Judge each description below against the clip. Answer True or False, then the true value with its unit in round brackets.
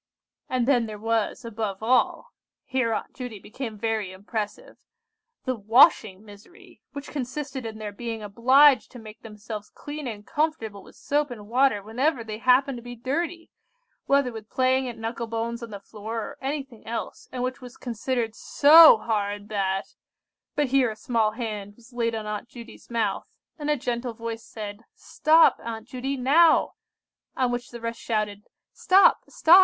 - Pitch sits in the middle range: False (235 Hz)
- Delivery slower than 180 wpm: True (165 wpm)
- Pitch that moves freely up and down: False (3.3 semitones)